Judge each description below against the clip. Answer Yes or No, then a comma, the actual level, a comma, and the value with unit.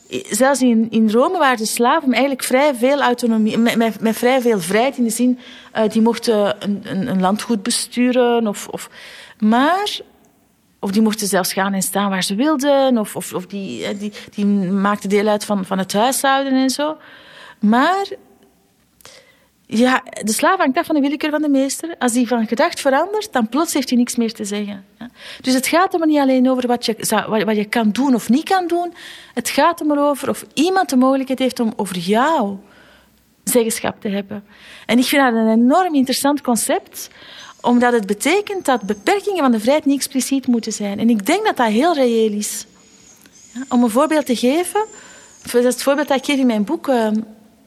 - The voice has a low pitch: No, high, 245 Hz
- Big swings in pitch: No, average, 4.2 semitones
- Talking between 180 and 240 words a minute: Yes, average, 195 wpm